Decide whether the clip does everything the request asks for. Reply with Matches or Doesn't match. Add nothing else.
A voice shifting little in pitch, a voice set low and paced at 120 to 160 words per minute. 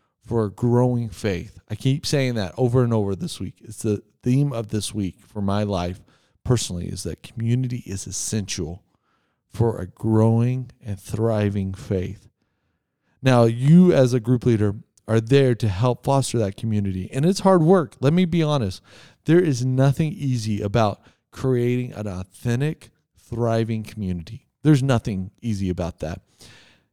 Doesn't match